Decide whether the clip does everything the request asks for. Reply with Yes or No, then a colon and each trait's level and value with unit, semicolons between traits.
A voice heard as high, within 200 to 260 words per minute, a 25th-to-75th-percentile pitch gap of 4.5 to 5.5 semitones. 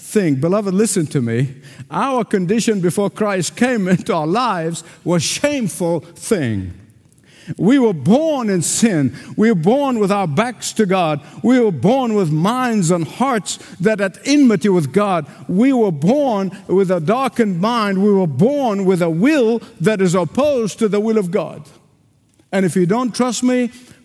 No: high, 200 Hz; average, 170 wpm; average, 5.1 semitones